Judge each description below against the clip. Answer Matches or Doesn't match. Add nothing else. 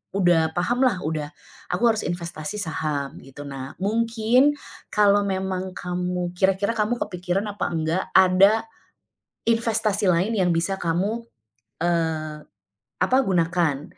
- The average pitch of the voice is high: Doesn't match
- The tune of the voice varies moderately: Matches